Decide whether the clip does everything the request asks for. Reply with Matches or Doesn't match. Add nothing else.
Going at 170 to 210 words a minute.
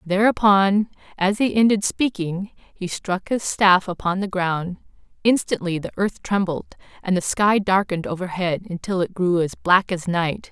Doesn't match